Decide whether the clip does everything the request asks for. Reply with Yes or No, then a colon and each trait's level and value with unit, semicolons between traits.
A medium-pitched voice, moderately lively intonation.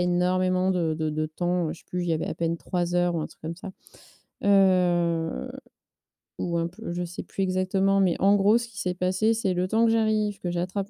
No: medium, 180 Hz; narrow, 2.2 semitones